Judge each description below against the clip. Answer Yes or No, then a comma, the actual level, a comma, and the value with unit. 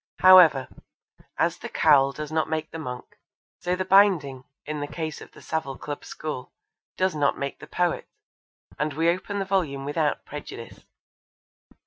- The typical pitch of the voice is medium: Yes, medium, 155 Hz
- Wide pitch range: No, average, 4.0 semitones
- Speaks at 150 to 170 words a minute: Yes, average, 160 wpm